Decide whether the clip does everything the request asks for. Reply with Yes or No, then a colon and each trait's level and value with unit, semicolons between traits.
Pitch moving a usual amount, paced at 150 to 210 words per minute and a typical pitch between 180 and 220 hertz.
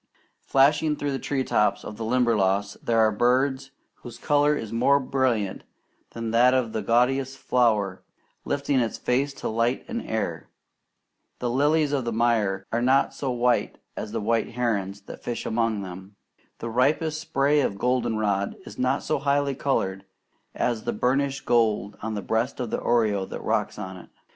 No: average, 4.0 semitones; average, 170 wpm; low, 120 Hz